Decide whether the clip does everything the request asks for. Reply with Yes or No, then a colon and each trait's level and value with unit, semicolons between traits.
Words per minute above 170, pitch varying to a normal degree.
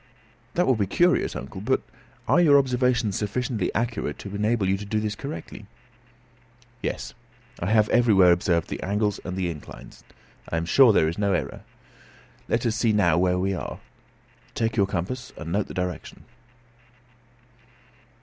No: average, 160 wpm; average, 4.5 semitones